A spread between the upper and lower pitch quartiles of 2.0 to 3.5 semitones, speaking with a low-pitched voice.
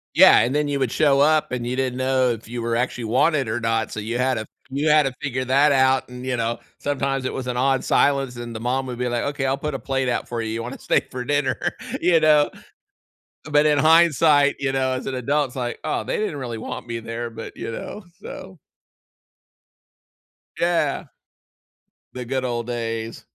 Yes: average, 3.0 semitones; low, 130 Hz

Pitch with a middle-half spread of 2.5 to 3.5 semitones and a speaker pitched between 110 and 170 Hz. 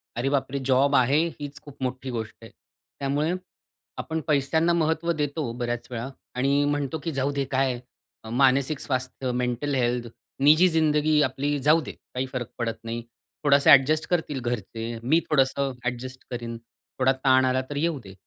Yes: average, 2.8 semitones; low, 135 Hz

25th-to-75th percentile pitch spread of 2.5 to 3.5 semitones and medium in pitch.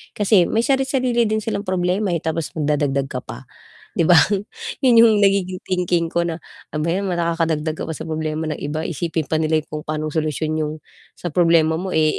Yes: average, 3.2 semitones; medium, 165 Hz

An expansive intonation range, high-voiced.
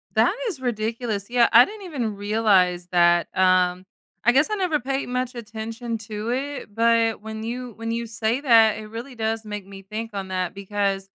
No: average, 3.2 semitones; high, 225 Hz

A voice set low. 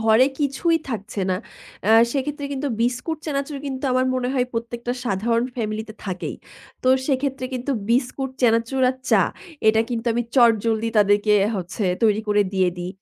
No: high, 235 Hz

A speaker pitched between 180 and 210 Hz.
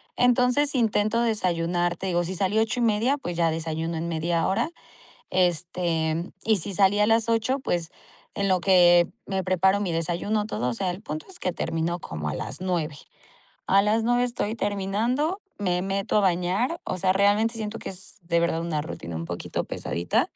Yes: medium, 185 Hz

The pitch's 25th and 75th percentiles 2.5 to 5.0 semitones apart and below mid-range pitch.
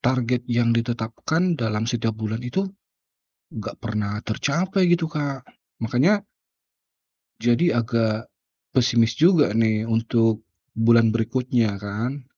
Yes: average, 2.8 semitones; low, 115 Hz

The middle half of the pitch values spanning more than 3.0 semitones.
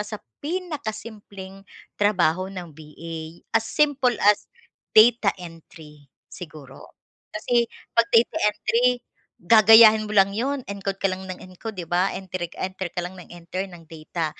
Yes: average, 4.3 semitones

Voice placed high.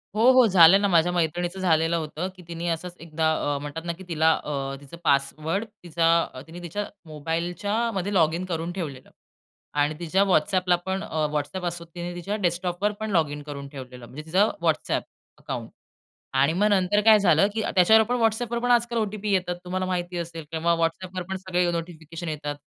No: medium, 175 Hz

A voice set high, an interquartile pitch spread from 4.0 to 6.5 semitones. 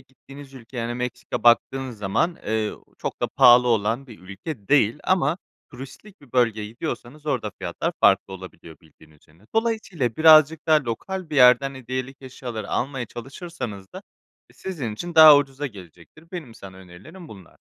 No: low, 125 Hz; wide, 5.5 semitones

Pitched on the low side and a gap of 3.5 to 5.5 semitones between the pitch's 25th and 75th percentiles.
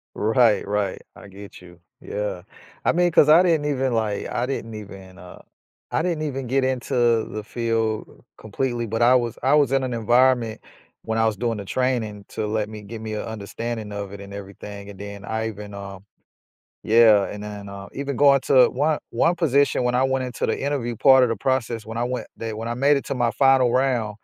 Yes: low, 115 Hz; average, 3.9 semitones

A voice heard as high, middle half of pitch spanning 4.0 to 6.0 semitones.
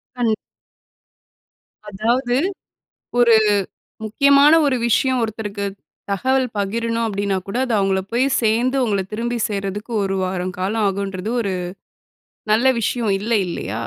No: high, 220 Hz; average, 3.6 semitones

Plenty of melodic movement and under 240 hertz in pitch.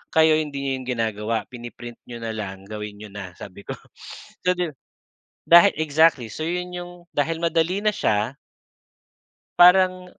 Yes: wide, 7.5 semitones; medium, 140 Hz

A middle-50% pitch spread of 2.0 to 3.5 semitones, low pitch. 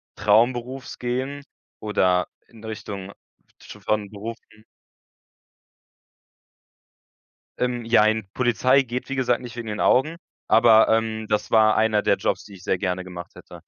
Yes: average, 2.8 semitones; low, 110 Hz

